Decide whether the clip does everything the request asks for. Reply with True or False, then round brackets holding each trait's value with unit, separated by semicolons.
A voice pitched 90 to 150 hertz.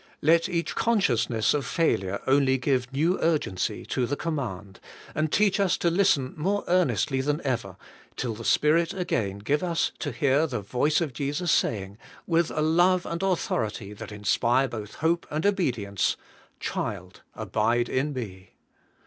True (140 Hz)